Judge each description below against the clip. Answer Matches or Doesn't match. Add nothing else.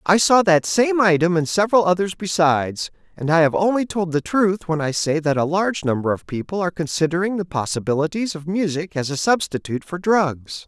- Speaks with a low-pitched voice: Doesn't match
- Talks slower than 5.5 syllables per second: Doesn't match